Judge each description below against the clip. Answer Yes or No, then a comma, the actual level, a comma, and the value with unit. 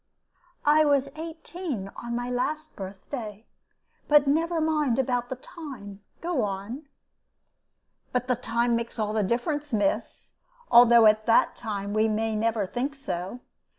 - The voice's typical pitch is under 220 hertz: No, high, 245 Hz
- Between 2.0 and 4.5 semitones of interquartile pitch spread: No, average, 5.2 semitones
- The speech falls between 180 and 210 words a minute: No, average, 140 wpm